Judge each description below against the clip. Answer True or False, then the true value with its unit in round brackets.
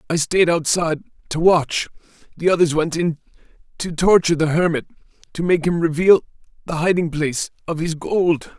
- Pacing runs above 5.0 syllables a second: True (5.4 syllables/s)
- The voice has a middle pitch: True (165 Hz)